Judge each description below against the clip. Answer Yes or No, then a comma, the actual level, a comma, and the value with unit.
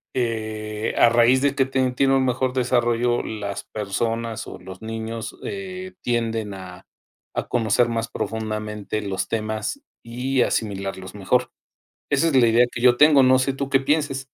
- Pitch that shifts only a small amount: No, average, 3.4 semitones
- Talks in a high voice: No, low, 115 Hz